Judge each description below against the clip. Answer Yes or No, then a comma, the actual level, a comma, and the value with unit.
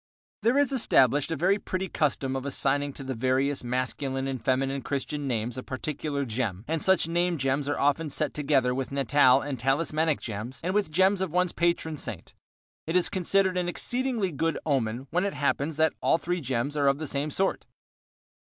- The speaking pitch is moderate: Yes, medium, 145 Hz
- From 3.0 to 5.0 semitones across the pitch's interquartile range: Yes, average, 4.3 semitones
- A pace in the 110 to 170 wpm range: No, average, 190 wpm